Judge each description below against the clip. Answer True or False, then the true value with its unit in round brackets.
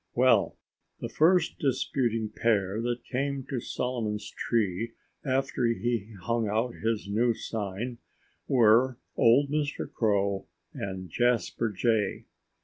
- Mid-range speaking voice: False (115 Hz)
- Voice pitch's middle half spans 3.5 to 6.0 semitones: False (3.0 semitones)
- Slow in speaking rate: True (115 wpm)